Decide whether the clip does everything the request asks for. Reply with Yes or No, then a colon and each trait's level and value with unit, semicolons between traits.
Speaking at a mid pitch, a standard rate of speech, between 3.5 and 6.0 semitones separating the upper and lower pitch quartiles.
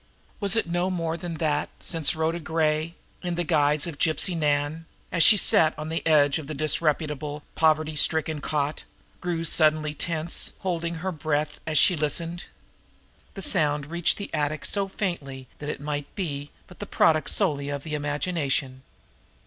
No: medium, 155 Hz; average, 165 wpm; narrow, 2.4 semitones